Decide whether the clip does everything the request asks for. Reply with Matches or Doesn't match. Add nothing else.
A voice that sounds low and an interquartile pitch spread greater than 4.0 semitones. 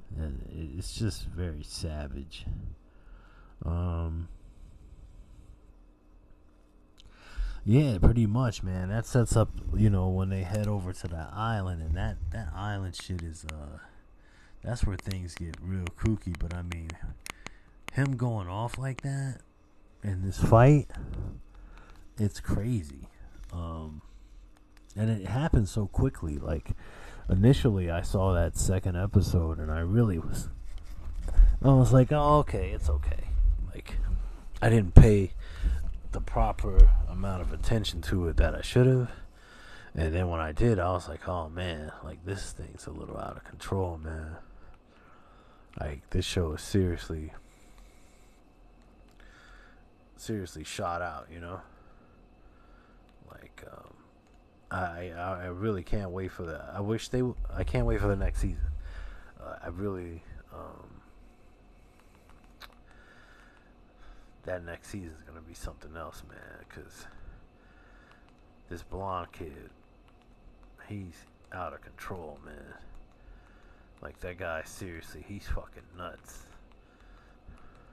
Matches